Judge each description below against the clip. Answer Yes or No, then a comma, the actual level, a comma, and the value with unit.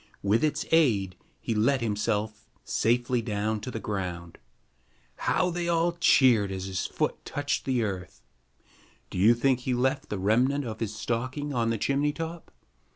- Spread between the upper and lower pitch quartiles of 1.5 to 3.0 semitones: No, average, 5.0 semitones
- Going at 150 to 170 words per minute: Yes, average, 160 wpm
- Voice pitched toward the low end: Yes, low, 120 Hz